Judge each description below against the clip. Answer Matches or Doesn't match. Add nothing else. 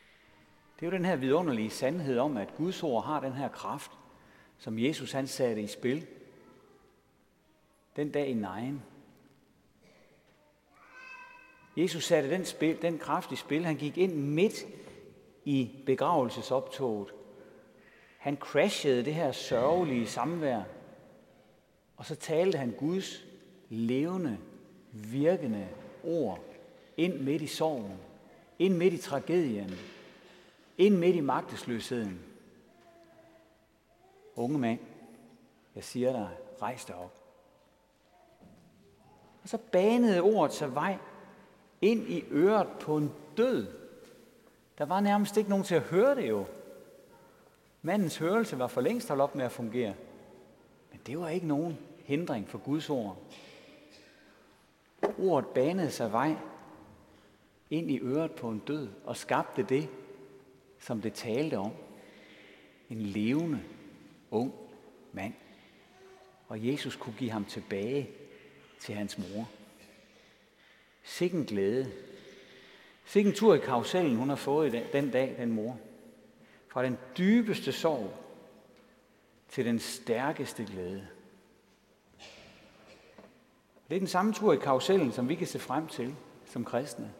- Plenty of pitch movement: Matches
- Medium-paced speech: Doesn't match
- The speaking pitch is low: Doesn't match